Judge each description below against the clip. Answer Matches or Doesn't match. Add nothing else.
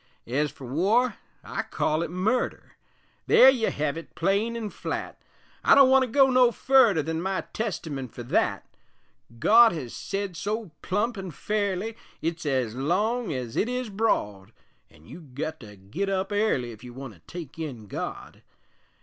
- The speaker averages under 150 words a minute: Doesn't match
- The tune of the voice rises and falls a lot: Matches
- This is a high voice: Doesn't match